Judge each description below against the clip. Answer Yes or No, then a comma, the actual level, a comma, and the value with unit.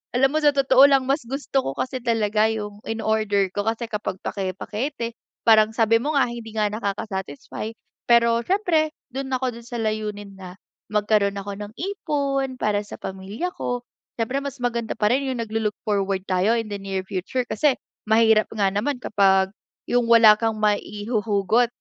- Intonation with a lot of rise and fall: No, average, 3.5 semitones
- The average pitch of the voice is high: Yes, high, 220 Hz